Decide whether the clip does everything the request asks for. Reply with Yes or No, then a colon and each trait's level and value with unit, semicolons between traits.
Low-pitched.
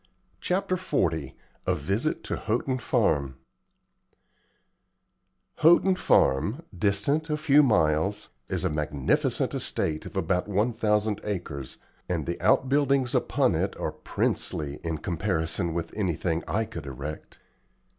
Yes: very low, 95 Hz